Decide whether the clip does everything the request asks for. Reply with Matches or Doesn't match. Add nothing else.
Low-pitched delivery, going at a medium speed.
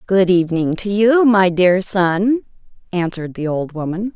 Doesn't match